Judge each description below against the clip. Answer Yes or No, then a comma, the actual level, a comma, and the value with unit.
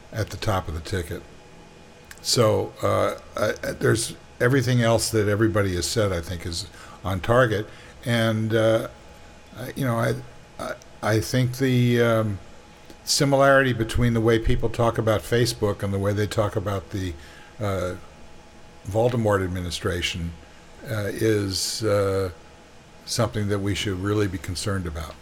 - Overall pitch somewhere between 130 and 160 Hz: No, low, 105 Hz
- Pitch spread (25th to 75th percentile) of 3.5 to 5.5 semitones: Yes, average, 3.9 semitones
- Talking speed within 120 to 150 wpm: Yes, average, 145 wpm